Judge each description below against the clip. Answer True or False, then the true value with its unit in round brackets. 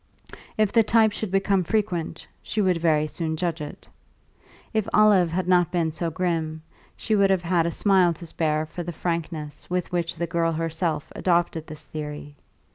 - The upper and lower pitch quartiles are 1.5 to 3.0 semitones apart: True (2.7 semitones)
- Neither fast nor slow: True (180 wpm)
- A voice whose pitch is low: False (170 Hz)